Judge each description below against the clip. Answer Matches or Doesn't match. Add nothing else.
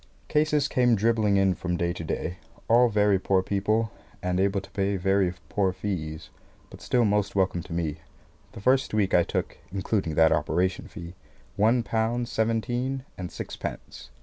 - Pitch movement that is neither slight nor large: Matches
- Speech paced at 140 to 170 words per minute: Matches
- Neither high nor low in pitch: Doesn't match